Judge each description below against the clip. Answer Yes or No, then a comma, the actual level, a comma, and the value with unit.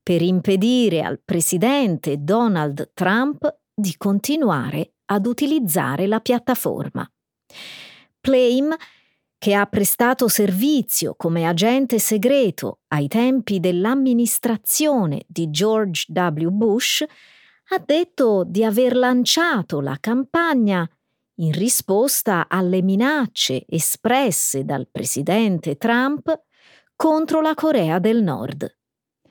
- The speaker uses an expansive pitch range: Yes, wide, 6.4 semitones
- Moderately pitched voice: No, high, 215 Hz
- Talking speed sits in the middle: No, slow, 95 wpm